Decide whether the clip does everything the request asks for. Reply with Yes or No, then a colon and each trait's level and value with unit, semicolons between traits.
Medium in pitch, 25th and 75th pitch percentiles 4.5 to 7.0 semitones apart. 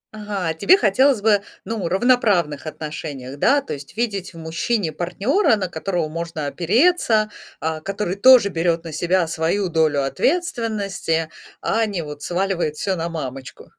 Yes: medium, 180 Hz; average, 4.9 semitones